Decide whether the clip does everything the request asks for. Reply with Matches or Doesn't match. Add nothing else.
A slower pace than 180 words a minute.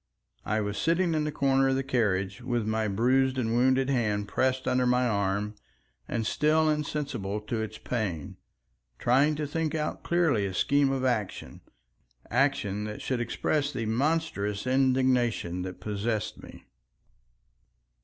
Matches